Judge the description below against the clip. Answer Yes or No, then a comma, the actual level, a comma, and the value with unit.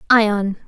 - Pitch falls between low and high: No, high, 210 Hz